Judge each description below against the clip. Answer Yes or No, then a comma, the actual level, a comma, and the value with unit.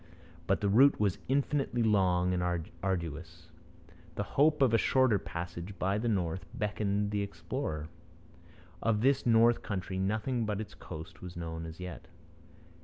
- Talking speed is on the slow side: No, average, 150 wpm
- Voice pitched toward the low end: Yes, low, 100 Hz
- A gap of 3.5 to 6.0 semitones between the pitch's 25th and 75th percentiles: Yes, average, 4.1 semitones